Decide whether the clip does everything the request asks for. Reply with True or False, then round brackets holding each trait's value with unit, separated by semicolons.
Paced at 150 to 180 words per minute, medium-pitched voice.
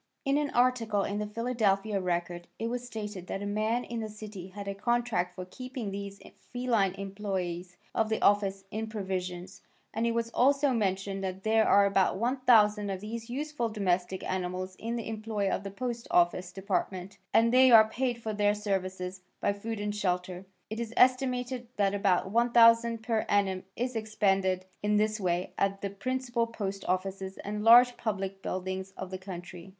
False (175 wpm; 205 Hz)